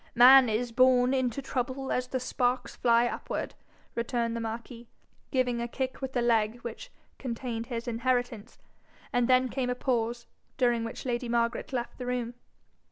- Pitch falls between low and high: No, high, 245 Hz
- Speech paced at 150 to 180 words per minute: Yes, average, 165 wpm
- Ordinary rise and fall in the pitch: No, narrow, 1.6 semitones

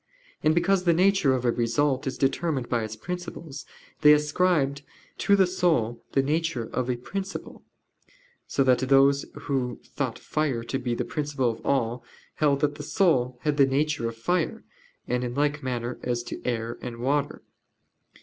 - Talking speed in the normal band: Yes, average, 170 wpm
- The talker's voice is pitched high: No, medium, 140 Hz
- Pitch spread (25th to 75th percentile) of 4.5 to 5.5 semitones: No, average, 3.9 semitones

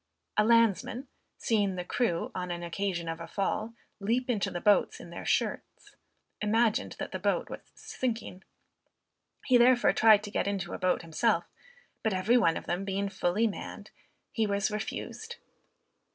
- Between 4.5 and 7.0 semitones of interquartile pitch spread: No, average, 3.9 semitones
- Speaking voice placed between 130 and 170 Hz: No, high, 205 Hz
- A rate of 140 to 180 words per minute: Yes, average, 165 wpm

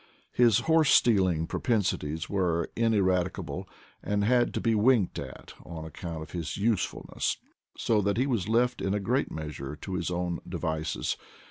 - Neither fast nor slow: Yes, average, 160 wpm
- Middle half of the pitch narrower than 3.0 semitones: No, wide, 5.5 semitones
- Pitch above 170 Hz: No, very low, 95 Hz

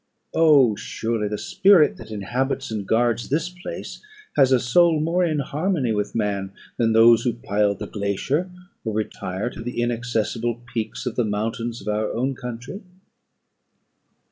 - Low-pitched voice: Yes, low, 120 Hz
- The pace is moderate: Yes, average, 155 wpm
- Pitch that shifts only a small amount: No, average, 4.3 semitones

